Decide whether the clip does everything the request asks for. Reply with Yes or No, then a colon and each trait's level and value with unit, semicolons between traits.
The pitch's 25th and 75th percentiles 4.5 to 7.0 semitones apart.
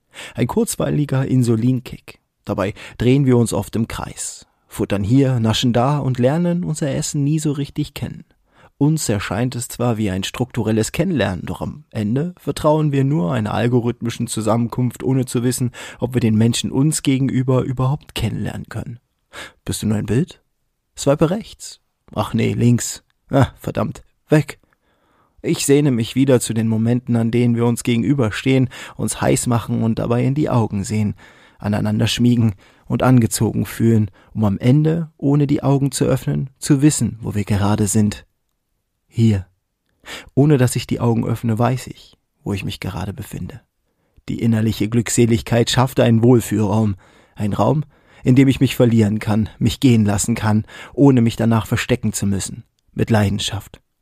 No: average, 3.6 semitones